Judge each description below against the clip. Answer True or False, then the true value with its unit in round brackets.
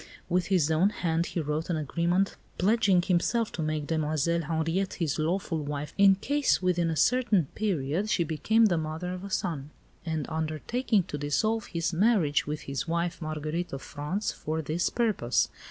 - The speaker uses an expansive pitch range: False (3.9 semitones)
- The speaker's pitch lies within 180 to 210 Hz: False (170 Hz)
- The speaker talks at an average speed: True (170 wpm)